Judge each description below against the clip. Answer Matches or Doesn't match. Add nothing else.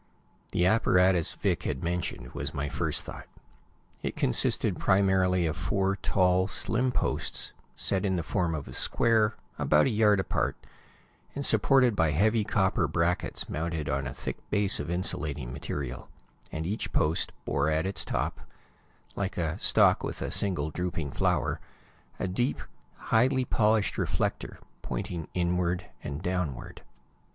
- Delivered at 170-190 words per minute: Doesn't match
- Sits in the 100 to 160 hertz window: Doesn't match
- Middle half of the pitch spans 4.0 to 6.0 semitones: Matches